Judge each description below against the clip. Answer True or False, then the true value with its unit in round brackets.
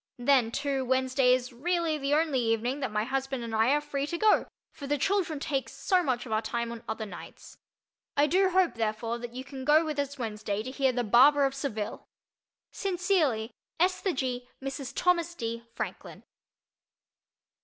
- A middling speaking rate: True (180 wpm)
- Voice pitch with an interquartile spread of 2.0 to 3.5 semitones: False (4.0 semitones)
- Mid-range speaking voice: False (265 Hz)